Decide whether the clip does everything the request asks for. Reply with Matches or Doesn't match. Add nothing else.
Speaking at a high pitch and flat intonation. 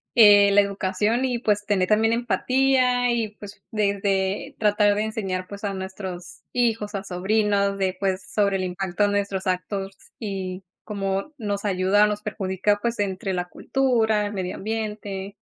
Matches